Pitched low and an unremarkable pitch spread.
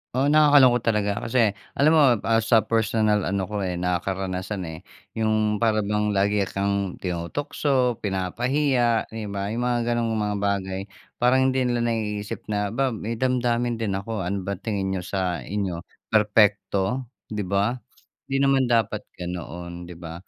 Yes: low, 105 Hz; average, 3.6 semitones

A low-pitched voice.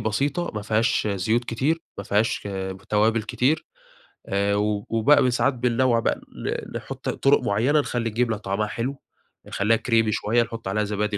Yes: low, 115 Hz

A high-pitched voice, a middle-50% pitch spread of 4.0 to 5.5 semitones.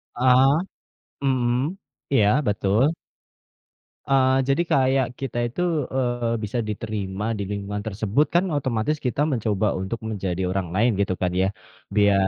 No: low, 110 Hz; average, 4.3 semitones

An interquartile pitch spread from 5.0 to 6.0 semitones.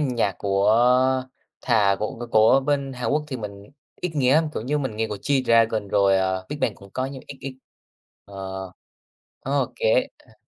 Yes: wide, 5.5 semitones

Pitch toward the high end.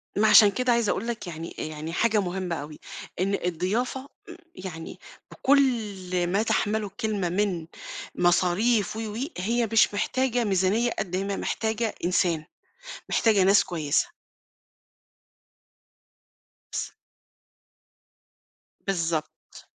Yes: high, 195 Hz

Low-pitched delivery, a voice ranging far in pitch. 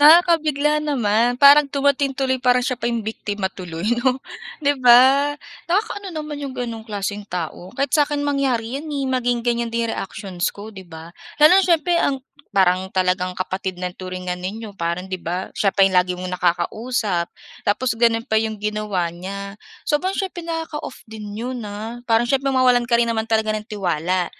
No: high, 230 Hz; wide, 6.3 semitones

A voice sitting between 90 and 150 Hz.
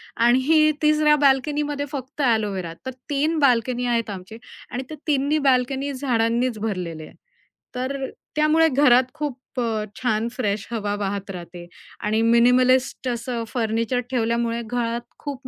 No: high, 245 Hz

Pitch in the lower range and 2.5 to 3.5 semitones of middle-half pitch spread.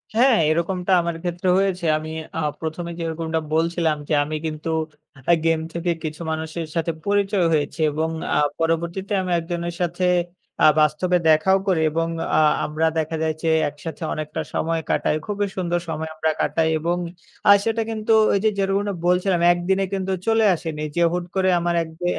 No: medium, 170 Hz; average, 2.8 semitones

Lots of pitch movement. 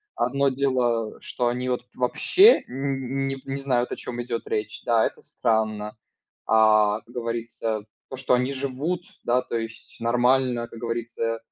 No: narrow, 2.5 semitones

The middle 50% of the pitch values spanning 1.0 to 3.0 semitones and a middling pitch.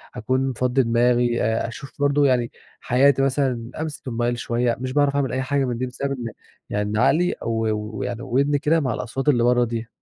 No: average, 2.7 semitones; low, 125 Hz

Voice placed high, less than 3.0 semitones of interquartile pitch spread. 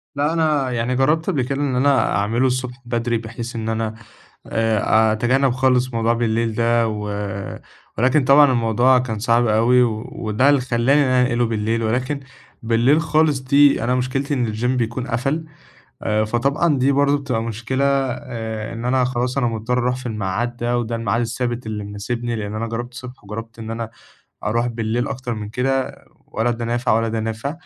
No: low, 120 Hz; narrow, 2.4 semitones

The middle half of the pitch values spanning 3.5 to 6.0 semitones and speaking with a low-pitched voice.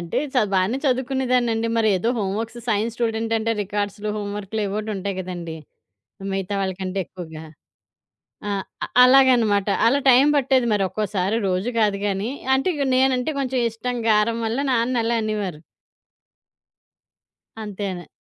No: average, 3.8 semitones; high, 215 Hz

